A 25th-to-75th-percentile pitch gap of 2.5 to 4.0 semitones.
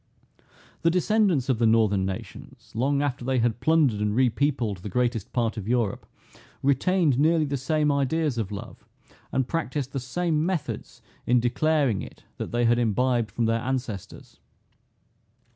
No: average, 4.5 semitones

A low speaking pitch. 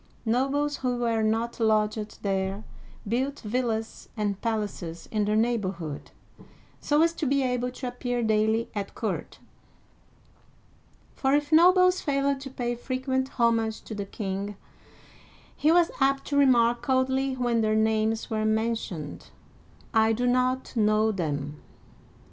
No: high, 230 Hz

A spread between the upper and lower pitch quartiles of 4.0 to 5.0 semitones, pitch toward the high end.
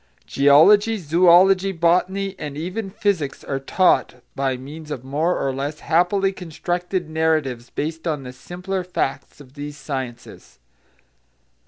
No: average, 4.6 semitones; medium, 160 Hz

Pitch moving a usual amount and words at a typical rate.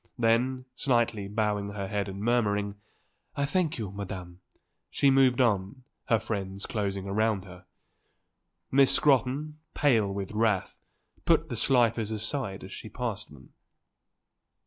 No: average, 4.3 semitones; slow, 130 wpm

